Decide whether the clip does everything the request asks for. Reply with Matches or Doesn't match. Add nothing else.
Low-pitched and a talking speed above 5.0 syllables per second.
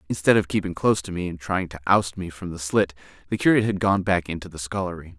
Matches